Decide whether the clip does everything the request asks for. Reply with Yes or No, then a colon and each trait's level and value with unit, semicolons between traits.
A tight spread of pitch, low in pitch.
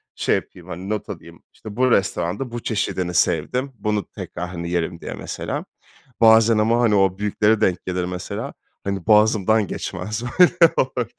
No: average, 3.8 semitones; low, 105 Hz